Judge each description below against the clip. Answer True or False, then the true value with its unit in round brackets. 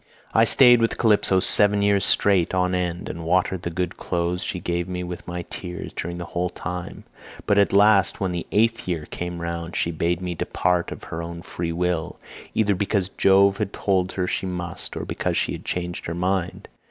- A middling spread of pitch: False (2.1 semitones)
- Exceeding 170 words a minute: True (200 wpm)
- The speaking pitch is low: True (90 Hz)